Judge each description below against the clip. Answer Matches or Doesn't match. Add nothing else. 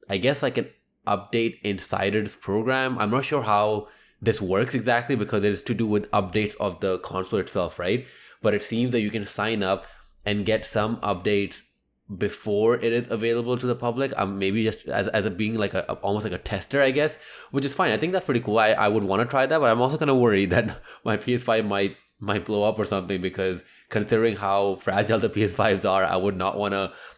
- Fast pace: Matches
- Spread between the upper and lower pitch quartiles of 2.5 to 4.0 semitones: Matches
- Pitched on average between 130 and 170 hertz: Doesn't match